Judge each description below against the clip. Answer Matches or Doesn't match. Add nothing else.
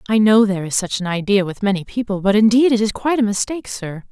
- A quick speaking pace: Matches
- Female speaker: Matches